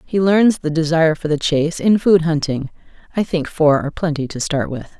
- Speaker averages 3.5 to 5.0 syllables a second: No, 5.5 syllables/s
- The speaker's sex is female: Yes, female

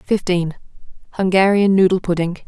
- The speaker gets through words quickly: No, slow, 75 wpm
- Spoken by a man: No, female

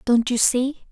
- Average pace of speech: Yes, average, 195 wpm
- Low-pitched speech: No, very high, 250 Hz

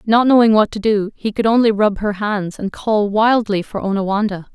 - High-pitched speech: Yes, high, 210 Hz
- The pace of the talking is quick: Yes, fast, 210 wpm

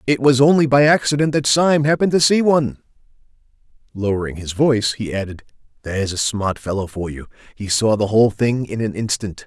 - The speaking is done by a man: Yes, male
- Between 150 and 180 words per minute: No, average, 190 wpm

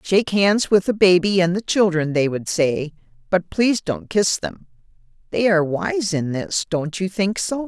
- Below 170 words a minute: No, average, 190 wpm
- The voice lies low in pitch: No, medium, 185 Hz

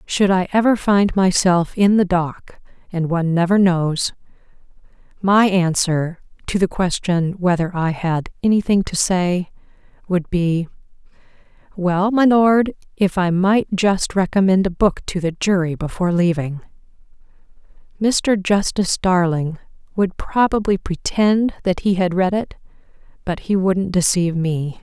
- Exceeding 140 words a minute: No, slow, 135 wpm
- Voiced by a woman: Yes, female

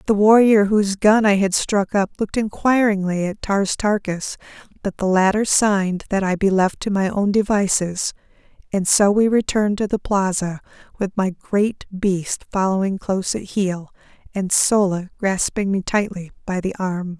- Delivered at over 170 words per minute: No, average, 165 wpm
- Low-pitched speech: No, high, 195 Hz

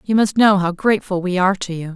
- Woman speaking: Yes, female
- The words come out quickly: Yes, fast, 275 wpm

